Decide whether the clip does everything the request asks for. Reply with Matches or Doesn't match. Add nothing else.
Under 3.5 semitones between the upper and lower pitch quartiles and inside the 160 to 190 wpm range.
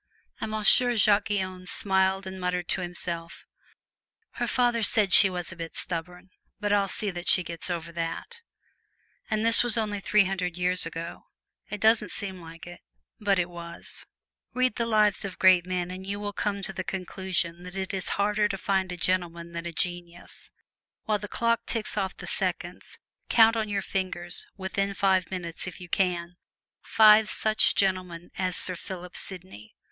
Matches